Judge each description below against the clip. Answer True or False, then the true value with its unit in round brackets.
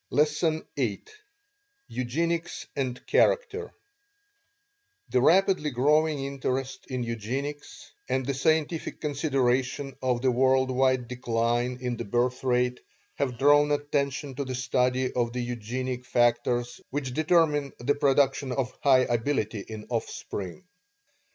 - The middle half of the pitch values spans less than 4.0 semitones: True (2.9 semitones)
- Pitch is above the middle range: False (130 Hz)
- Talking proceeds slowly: True (120 wpm)